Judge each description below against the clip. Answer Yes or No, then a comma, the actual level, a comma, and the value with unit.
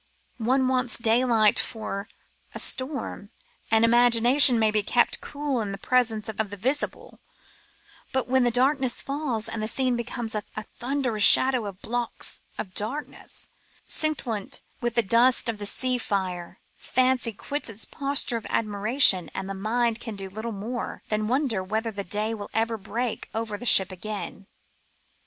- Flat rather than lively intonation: No, average, 3.1 semitones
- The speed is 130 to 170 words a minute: Yes, average, 155 wpm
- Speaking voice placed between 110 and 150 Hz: No, high, 230 Hz